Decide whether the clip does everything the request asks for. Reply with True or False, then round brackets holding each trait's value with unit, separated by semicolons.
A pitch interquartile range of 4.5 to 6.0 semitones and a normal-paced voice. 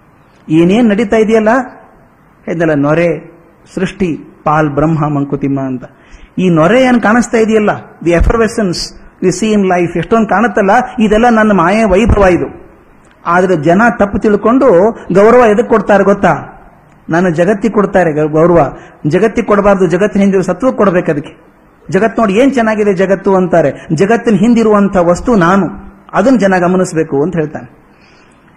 False (4.8 semitones; 125 wpm)